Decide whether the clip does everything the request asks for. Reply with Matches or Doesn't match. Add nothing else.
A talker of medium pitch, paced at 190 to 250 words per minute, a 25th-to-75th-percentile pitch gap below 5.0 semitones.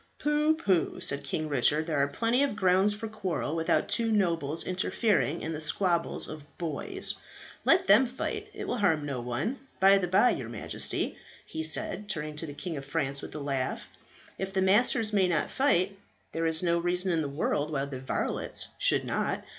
Doesn't match